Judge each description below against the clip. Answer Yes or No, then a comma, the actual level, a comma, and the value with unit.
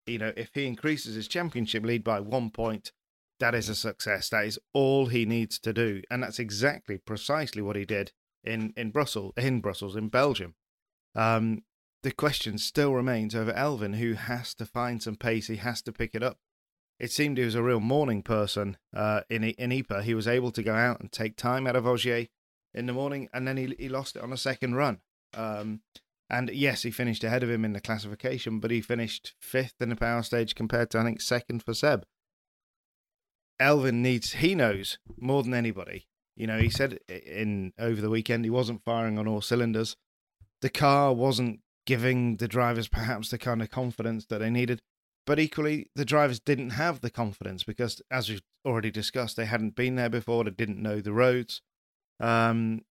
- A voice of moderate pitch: No, low, 115 Hz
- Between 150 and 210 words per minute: Yes, average, 200 wpm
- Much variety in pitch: No, narrow, 2.4 semitones